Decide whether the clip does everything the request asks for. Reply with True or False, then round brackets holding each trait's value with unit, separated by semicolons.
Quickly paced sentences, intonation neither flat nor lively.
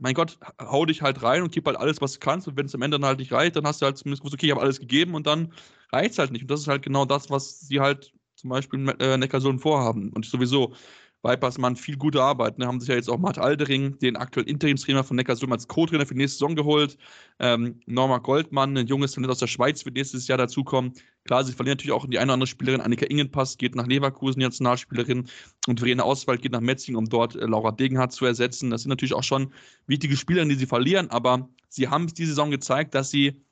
False (255 wpm; 2.0 semitones)